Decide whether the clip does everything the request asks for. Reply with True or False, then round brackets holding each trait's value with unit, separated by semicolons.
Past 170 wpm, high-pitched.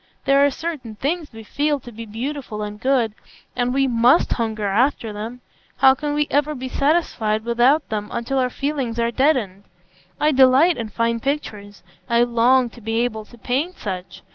True (180 wpm; 245 Hz)